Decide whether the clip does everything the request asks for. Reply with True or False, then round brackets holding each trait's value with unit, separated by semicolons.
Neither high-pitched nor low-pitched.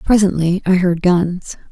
True (180 Hz)